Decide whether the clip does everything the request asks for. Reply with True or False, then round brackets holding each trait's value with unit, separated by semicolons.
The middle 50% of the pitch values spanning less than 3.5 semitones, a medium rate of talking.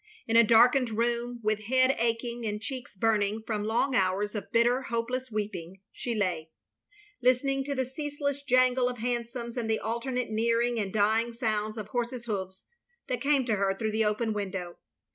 True (2.8 semitones; 180 wpm)